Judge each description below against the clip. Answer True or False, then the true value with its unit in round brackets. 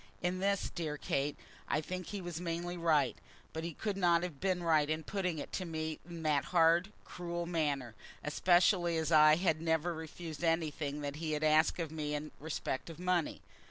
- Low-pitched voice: False (165 Hz)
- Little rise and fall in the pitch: True (2.3 semitones)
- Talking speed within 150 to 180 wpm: False (195 wpm)